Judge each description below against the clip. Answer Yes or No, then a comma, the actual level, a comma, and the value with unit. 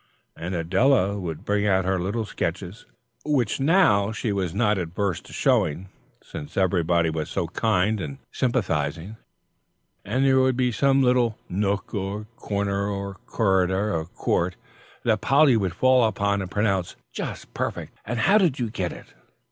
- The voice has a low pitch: Yes, low, 100 Hz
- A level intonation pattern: No, average, 4.2 semitones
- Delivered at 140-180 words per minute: Yes, average, 155 wpm